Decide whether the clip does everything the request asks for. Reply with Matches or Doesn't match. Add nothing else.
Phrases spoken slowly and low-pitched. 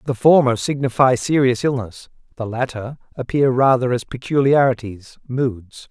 Matches